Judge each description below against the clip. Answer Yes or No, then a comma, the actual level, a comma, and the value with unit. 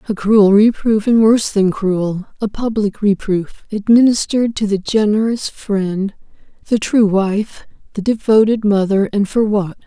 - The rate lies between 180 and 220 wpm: No, average, 140 wpm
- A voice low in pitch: No, high, 210 Hz